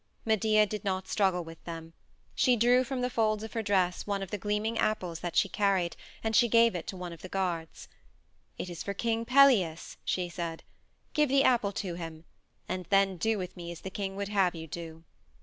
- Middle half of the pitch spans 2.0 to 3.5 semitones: No, average, 4.0 semitones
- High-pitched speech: Yes, high, 195 Hz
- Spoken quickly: Yes, fast, 215 wpm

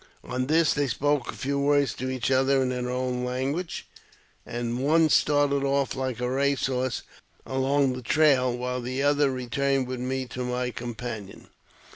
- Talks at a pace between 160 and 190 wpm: Yes, average, 175 wpm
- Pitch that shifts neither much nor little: No, narrow, 2.0 semitones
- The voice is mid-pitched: No, low, 130 Hz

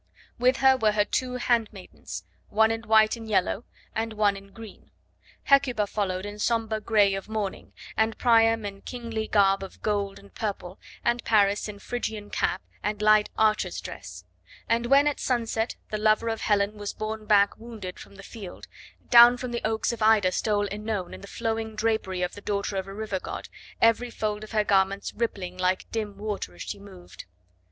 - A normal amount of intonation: No, narrow, 2.1 semitones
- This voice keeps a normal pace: Yes, average, 185 wpm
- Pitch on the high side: Yes, high, 215 Hz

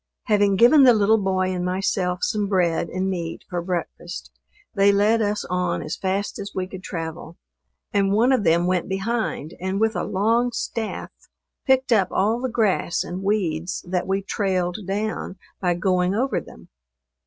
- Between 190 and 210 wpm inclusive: No, average, 170 wpm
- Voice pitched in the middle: No, high, 195 Hz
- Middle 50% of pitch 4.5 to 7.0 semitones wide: No, average, 3.0 semitones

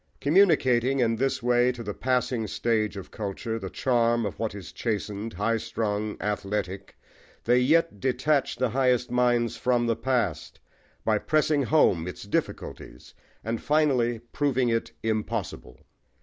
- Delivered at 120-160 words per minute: Yes, average, 140 wpm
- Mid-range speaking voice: No, low, 115 Hz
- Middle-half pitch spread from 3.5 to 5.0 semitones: No, average, 3.1 semitones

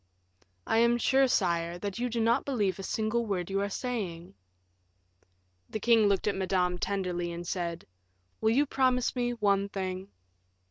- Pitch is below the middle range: No, high, 200 Hz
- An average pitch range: Yes, average, 4.4 semitones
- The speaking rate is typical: Yes, average, 165 wpm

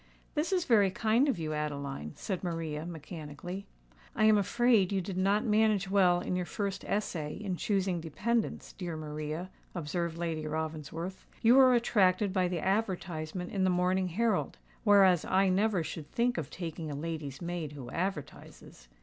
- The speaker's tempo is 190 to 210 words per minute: No, average, 165 wpm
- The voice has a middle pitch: Yes, medium, 180 Hz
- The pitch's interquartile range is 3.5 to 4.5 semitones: Yes, average, 4.1 semitones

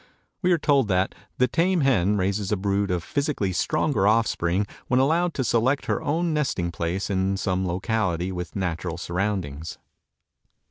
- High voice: No, low, 100 Hz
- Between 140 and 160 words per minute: Yes, average, 155 wpm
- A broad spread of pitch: Yes, wide, 6.8 semitones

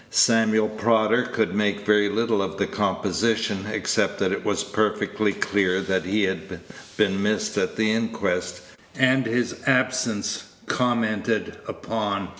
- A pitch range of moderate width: No, narrow, 2.2 semitones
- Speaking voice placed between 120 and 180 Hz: No, low, 110 Hz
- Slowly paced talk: Yes, slow, 130 wpm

